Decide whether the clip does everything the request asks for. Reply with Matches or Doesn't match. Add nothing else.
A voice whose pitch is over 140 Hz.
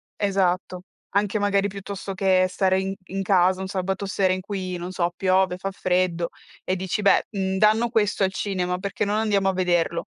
Matches